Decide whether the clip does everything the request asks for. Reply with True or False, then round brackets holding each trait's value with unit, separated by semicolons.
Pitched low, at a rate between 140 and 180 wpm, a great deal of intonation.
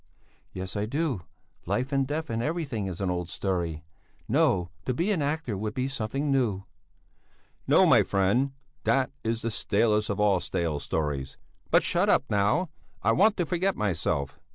True (110 Hz; 170 wpm; 6.8 semitones)